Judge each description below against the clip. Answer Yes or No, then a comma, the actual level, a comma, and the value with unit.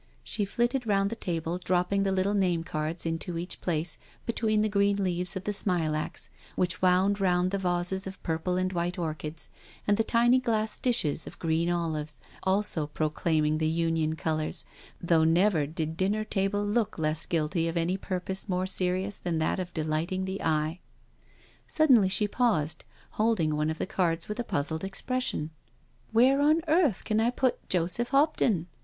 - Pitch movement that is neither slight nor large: Yes, average, 4.0 semitones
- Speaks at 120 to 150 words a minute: No, average, 175 wpm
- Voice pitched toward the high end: No, medium, 180 Hz